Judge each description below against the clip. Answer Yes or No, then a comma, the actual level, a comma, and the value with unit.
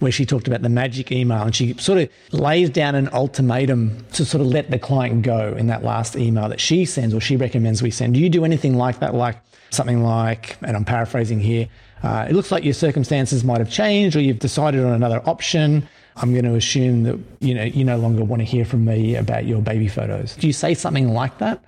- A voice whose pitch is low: Yes, low, 125 Hz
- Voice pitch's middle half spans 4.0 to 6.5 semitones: No, average, 3.3 semitones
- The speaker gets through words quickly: Yes, fast, 240 wpm